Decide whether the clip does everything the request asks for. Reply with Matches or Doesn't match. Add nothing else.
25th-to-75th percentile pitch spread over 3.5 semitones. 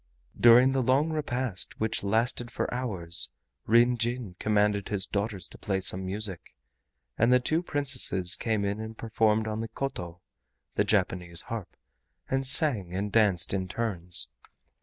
Matches